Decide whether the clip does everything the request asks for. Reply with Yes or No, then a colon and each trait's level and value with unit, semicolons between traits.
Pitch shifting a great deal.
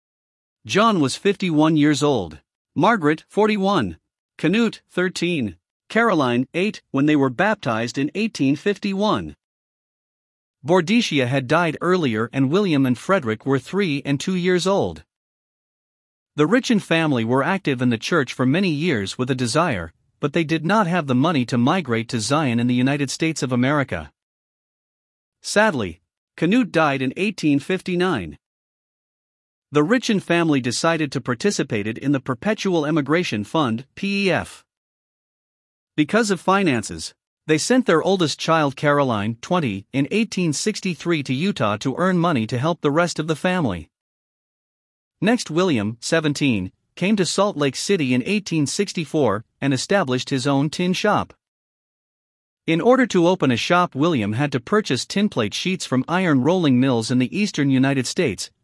Yes: wide, 6.2 semitones